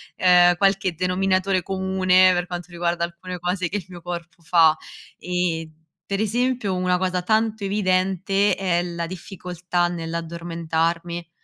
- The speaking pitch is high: No, medium, 180 Hz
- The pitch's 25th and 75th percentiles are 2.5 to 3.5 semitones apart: No, narrow, 1.8 semitones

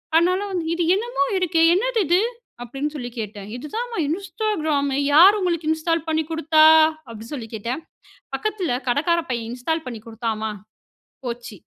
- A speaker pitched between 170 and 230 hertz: No, very high, 315 Hz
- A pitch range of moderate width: No, wide, 6.6 semitones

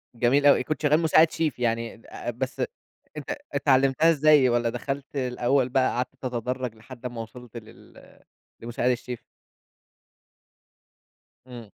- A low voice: Yes, low, 125 Hz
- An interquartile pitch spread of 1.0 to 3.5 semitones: Yes, average, 2.8 semitones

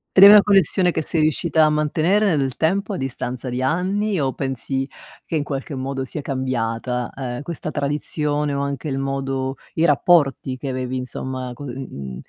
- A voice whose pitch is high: No, medium, 140 Hz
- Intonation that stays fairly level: No, average, 3.5 semitones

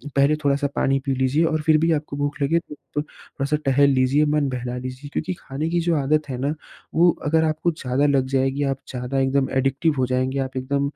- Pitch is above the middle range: No, medium, 140 Hz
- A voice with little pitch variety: Yes, narrow, 2.3 semitones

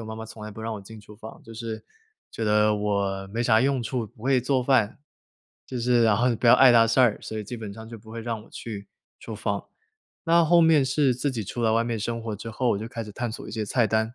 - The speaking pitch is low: Yes, low, 115 Hz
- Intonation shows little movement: Yes, narrow, 2.2 semitones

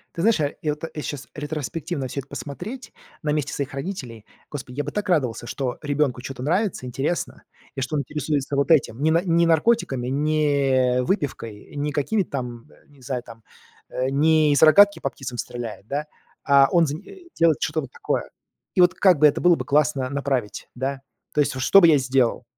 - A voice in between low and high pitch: Yes, medium, 145 Hz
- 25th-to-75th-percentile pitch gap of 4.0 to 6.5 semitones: No, average, 3.3 semitones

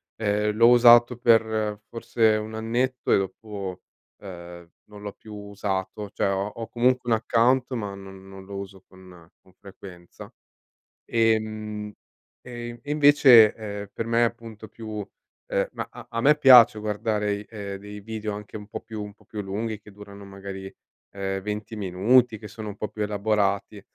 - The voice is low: Yes, low, 105 Hz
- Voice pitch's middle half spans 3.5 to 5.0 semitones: No, narrow, 2.4 semitones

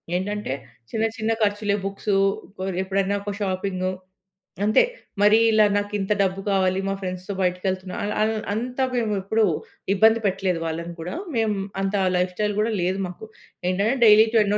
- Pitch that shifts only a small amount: Yes, narrow, 2.3 semitones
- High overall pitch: Yes, high, 200 Hz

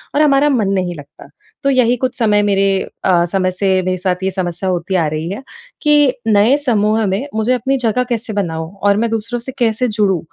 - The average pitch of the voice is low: No, high, 205 Hz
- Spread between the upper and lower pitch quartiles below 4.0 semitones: No, average, 4.6 semitones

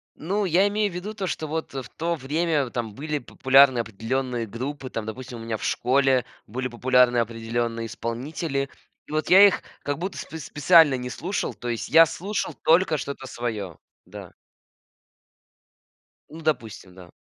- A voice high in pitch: No, low, 135 Hz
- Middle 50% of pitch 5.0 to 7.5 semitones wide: Yes, wide, 5.4 semitones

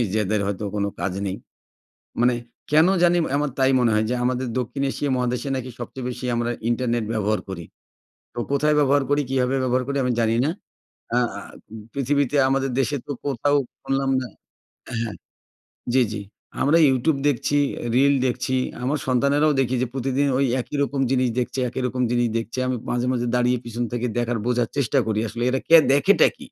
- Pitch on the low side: Yes, low, 125 Hz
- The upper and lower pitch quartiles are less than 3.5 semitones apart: Yes, average, 2.7 semitones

